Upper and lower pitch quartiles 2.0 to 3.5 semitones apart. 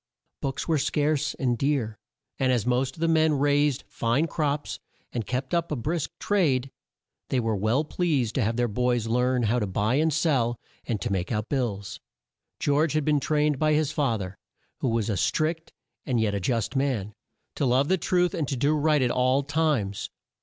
No: average, 4.5 semitones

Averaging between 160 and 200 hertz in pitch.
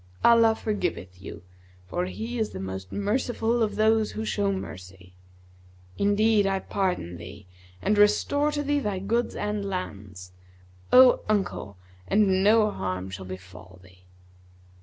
Yes: high, 190 Hz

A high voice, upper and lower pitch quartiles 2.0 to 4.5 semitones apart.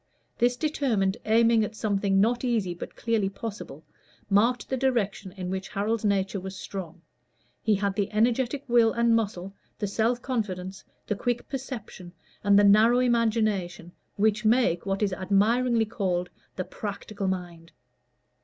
Yes: high, 210 Hz; average, 3.4 semitones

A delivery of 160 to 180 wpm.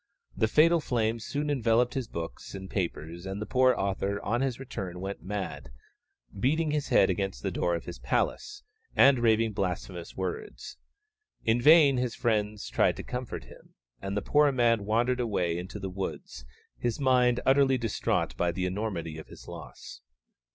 Yes: average, 170 wpm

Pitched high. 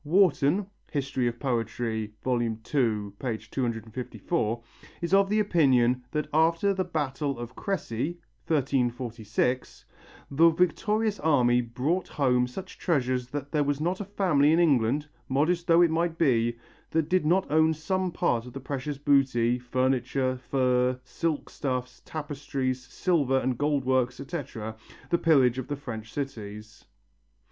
No: low, 135 Hz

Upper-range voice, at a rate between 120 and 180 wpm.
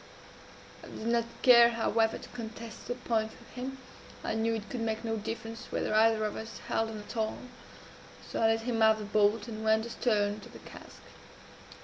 No: high, 225 Hz; average, 200 wpm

